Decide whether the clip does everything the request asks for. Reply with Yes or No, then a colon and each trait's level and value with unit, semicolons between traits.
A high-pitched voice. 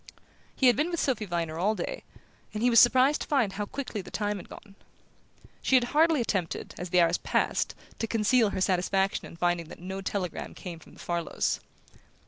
Yes: high, 205 Hz